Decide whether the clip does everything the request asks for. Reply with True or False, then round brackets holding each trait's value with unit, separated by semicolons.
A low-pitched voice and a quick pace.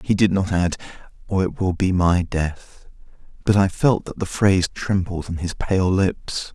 False (95 Hz; 195 wpm)